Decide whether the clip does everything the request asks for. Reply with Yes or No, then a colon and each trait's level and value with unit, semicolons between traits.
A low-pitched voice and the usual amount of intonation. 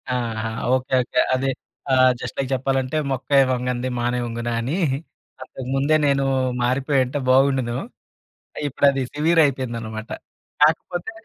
No: low, 130 Hz; narrow, 2.1 semitones